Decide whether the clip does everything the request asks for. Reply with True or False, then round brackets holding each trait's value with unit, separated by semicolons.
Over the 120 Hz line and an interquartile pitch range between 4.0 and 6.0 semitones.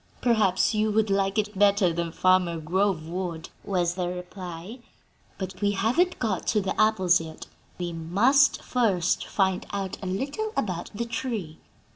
False (190 Hz; 3.4 semitones)